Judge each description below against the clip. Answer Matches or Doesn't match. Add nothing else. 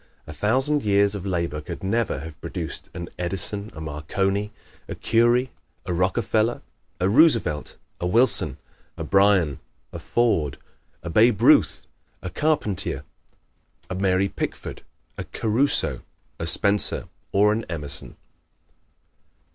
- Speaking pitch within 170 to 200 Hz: Doesn't match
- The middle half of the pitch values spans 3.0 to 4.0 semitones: Doesn't match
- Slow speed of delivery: Matches